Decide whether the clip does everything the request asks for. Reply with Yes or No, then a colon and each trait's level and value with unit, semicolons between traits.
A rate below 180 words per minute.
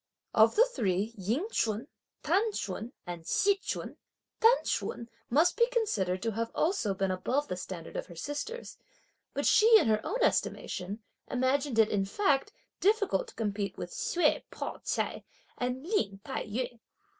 Yes: average, 160 wpm